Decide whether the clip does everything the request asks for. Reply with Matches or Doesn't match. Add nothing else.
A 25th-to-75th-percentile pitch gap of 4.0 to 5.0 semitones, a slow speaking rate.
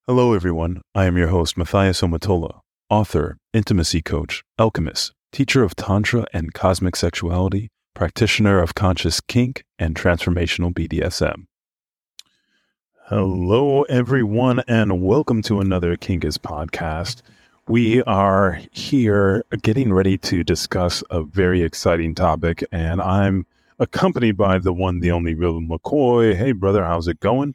Matches